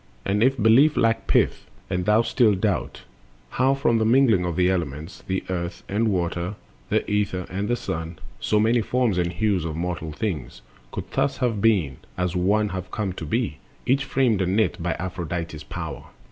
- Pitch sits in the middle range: No, very low, 95 Hz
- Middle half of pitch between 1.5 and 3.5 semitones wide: No, average, 4.4 semitones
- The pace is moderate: Yes, average, 180 wpm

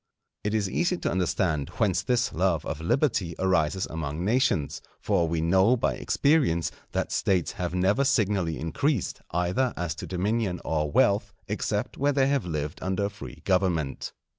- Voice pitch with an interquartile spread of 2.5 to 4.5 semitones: No, average, 5.1 semitones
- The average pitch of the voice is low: Yes, very low, 95 Hz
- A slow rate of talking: No, average, 165 wpm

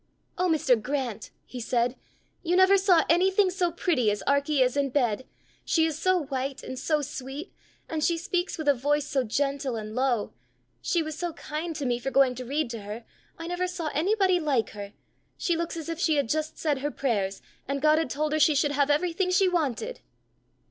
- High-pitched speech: Yes, very high, 295 Hz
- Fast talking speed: Yes, fast, 210 wpm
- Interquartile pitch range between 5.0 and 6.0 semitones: No, average, 4.5 semitones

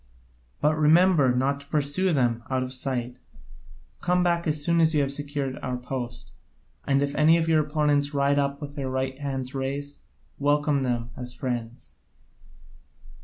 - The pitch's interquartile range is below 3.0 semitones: Yes, narrow, 2.5 semitones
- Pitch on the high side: No, medium, 140 Hz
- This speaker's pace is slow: No, average, 165 wpm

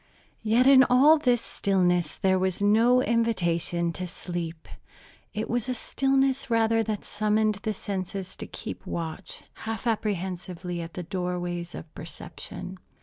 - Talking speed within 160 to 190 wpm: No, average, 140 wpm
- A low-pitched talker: No, high, 195 Hz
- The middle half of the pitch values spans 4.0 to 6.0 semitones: Yes, average, 4.4 semitones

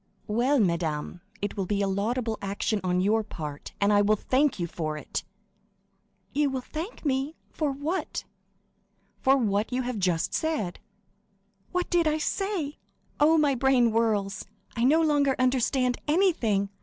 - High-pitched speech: Yes, high, 245 Hz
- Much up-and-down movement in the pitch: Yes, wide, 6.4 semitones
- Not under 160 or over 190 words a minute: No, average, 150 wpm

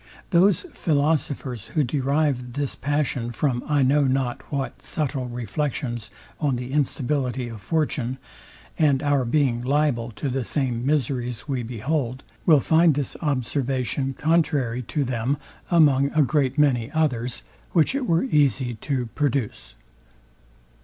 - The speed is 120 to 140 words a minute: Yes, slow, 135 wpm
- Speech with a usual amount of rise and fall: Yes, average, 3.2 semitones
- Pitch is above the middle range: No, low, 135 Hz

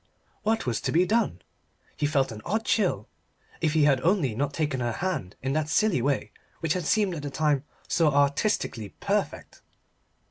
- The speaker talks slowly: No, average, 180 wpm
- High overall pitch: No, medium, 150 Hz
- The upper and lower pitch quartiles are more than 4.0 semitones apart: Yes, average, 5.3 semitones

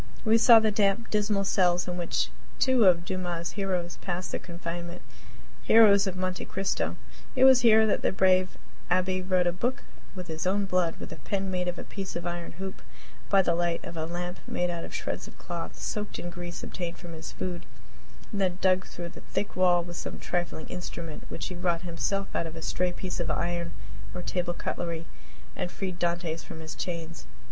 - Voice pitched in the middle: Yes, medium, 180 Hz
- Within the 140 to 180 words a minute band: No, fast, 205 wpm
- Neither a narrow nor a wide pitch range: No, narrow, 1.9 semitones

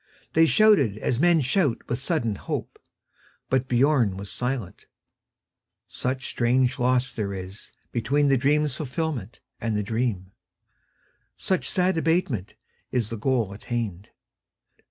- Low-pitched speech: Yes, low, 125 Hz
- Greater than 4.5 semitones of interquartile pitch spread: Yes, average, 5.0 semitones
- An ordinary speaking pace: No, slow, 115 wpm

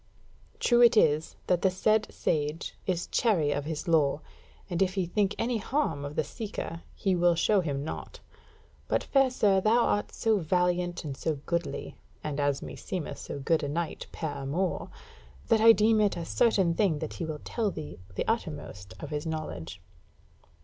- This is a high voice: No, medium, 175 Hz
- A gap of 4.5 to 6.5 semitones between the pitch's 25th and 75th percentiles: Yes, wide, 5.5 semitones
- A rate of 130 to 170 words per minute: No, average, 180 wpm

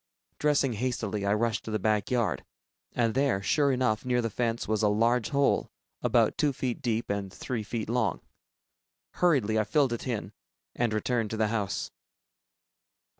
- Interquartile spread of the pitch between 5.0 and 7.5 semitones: No, average, 2.8 semitones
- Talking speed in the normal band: Yes, average, 170 wpm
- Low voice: Yes, low, 115 Hz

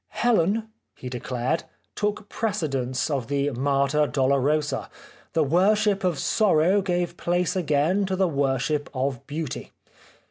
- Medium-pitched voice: Yes, medium, 155 Hz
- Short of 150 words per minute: Yes, slow, 135 wpm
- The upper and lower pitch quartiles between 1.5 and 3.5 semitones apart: No, average, 5.3 semitones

